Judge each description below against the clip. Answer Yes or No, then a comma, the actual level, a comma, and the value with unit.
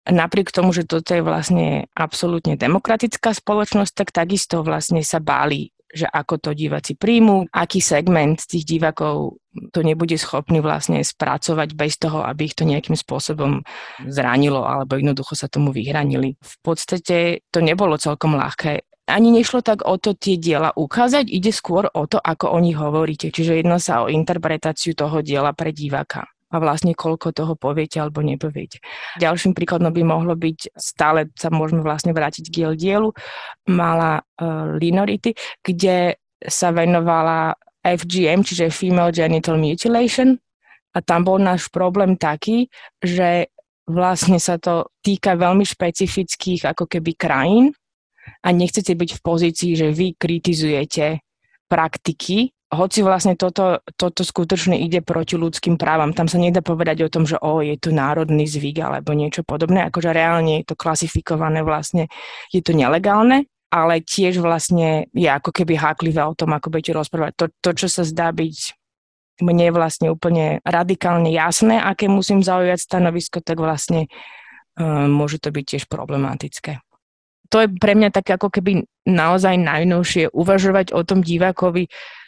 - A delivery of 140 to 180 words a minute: Yes, average, 155 wpm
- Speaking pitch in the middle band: Yes, medium, 170 Hz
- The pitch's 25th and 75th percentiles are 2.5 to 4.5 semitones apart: Yes, average, 2.8 semitones